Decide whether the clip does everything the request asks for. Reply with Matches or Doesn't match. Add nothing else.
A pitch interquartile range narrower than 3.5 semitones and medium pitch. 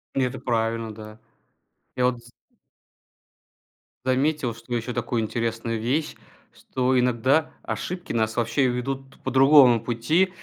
Doesn't match